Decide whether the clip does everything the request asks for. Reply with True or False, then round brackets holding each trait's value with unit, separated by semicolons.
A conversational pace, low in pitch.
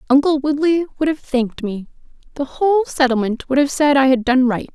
False (190 wpm; 275 Hz)